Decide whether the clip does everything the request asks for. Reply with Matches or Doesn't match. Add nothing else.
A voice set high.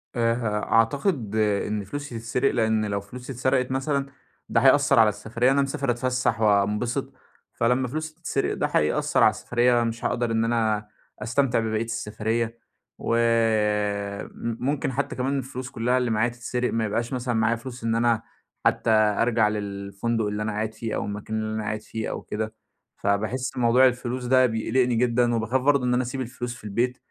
Doesn't match